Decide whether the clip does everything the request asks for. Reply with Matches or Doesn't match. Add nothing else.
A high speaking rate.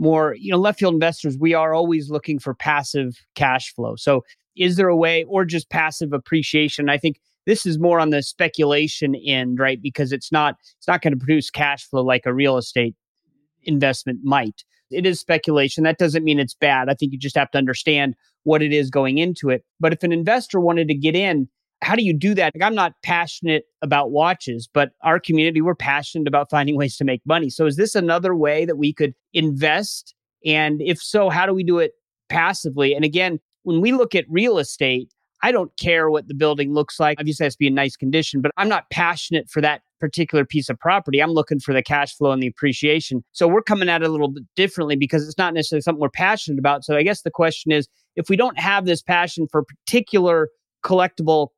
Matches